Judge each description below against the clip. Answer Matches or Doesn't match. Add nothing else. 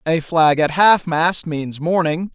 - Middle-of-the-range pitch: Matches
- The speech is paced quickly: Doesn't match